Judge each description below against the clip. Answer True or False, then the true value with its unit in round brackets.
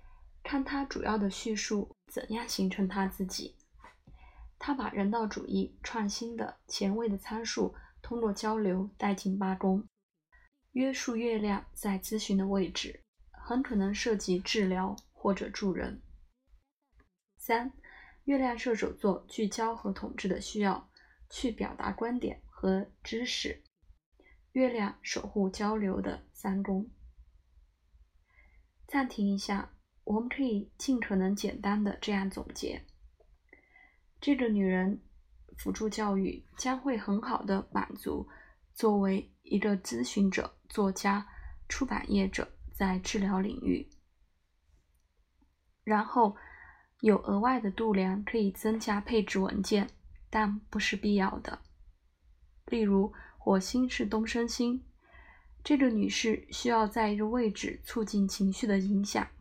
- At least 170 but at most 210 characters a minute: True (190 characters per minute)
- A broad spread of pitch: False (3.0 semitones)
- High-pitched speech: True (205 Hz)